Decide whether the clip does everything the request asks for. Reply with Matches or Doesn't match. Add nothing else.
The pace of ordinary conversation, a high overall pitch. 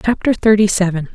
Matches